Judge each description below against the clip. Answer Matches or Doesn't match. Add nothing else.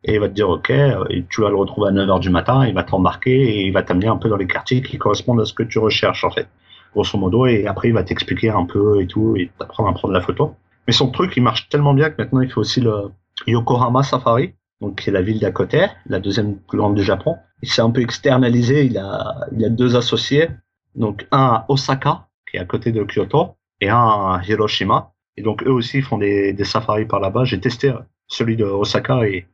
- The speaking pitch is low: Matches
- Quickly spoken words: Matches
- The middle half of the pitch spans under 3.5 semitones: Doesn't match